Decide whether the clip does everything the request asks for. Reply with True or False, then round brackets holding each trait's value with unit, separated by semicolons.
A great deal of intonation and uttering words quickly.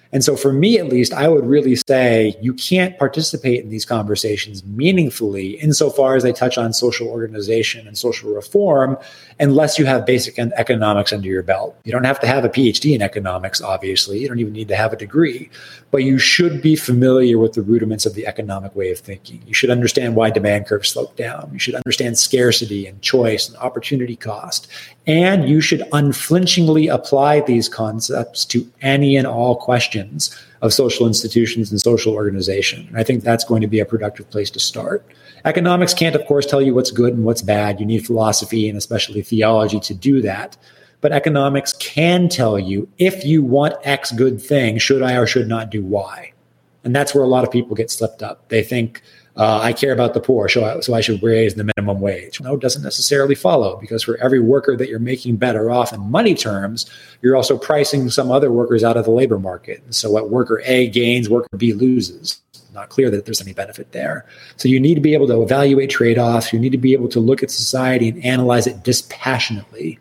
False (3.7 semitones; 210 wpm)